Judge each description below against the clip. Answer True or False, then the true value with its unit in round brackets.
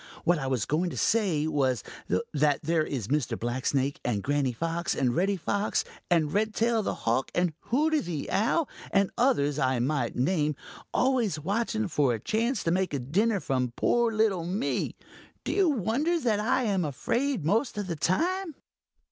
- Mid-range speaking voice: True (175 Hz)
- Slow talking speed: False (175 wpm)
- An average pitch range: False (7.7 semitones)